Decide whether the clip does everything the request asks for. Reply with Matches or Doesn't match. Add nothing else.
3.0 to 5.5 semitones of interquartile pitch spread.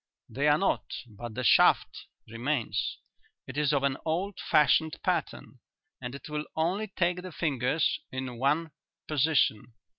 Matches